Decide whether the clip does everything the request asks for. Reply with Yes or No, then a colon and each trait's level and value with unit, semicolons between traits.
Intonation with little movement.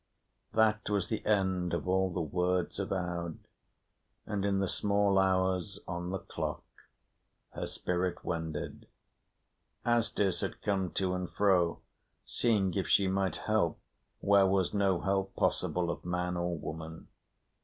Yes: narrow, 2.0 semitones